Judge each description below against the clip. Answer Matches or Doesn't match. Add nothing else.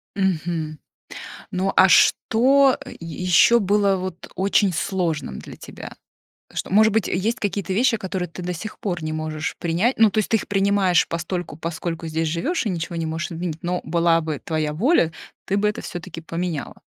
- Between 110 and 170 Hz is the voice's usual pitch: Doesn't match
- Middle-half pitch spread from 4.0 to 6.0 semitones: Doesn't match